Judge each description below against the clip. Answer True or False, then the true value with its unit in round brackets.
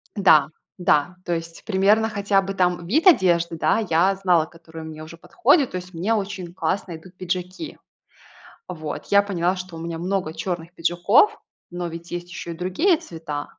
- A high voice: False (180 Hz)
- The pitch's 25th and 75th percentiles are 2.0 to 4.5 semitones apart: True (2.7 semitones)